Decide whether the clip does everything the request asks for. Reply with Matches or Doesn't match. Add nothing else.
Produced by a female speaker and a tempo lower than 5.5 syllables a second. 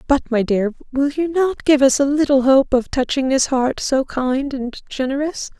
Matches